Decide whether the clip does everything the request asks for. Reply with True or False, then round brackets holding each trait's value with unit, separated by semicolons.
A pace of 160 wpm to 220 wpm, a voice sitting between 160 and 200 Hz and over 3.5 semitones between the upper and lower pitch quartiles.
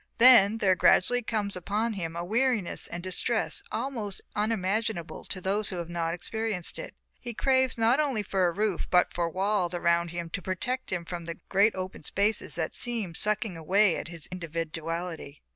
True (175 wpm; 190 Hz; 4.2 semitones)